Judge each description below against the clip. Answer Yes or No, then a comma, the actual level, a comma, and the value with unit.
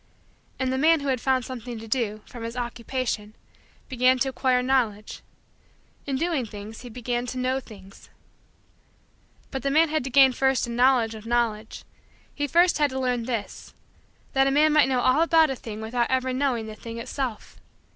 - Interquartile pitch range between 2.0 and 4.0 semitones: Yes, narrow, 2.6 semitones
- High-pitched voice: Yes, very high, 255 Hz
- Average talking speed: Yes, average, 185 wpm